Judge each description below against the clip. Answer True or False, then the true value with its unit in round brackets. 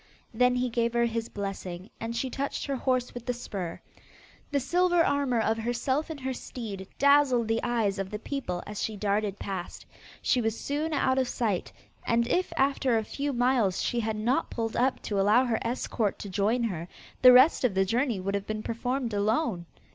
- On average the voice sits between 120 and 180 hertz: False (235 Hz)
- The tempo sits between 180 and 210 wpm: True (200 wpm)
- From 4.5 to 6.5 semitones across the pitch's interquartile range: False (3.8 semitones)